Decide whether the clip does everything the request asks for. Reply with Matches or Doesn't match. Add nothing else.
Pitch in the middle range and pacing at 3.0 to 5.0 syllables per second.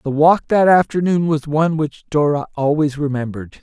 Doesn't match